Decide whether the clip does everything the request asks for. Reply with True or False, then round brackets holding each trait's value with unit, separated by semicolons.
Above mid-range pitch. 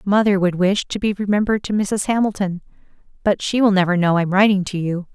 True (195 Hz)